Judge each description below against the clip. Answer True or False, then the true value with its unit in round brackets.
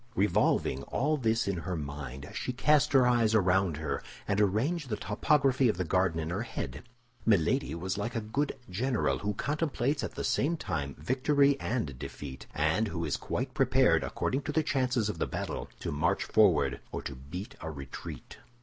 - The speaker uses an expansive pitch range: True (8.1 semitones)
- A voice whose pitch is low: True (105 Hz)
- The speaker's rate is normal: True (185 wpm)